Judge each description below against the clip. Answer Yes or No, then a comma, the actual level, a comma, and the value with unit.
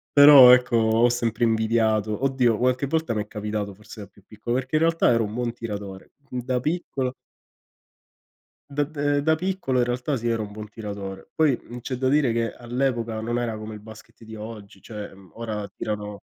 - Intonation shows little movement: No, average, 3.2 semitones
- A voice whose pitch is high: No, low, 115 Hz